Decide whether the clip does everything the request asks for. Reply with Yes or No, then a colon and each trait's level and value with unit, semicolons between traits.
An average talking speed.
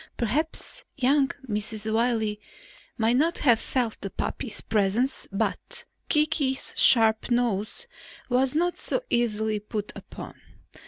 No: slow, 115 wpm